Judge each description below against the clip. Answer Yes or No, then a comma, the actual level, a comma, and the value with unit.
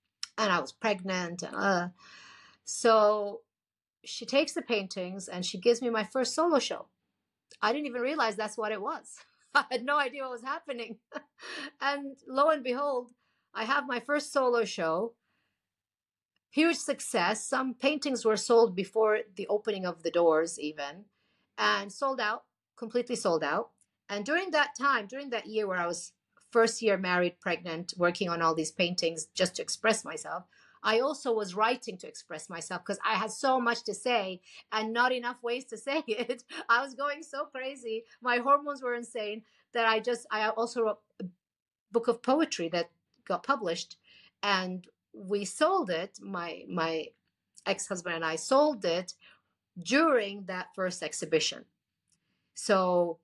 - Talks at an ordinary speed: Yes, average, 165 wpm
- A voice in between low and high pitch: No, high, 220 Hz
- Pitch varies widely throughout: Yes, wide, 6.0 semitones